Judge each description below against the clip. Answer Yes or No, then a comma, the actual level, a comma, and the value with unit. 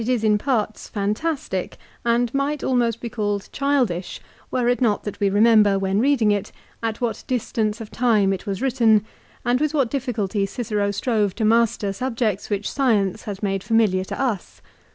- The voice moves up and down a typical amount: Yes, average, 3.3 semitones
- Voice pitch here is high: Yes, high, 220 Hz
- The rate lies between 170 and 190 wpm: Yes, average, 175 wpm